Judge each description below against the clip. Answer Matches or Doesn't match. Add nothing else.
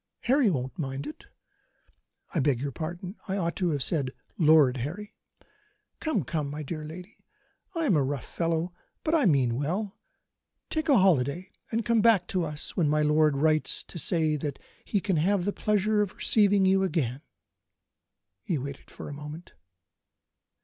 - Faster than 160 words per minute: Matches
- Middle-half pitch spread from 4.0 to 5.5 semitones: Matches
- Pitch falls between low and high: Matches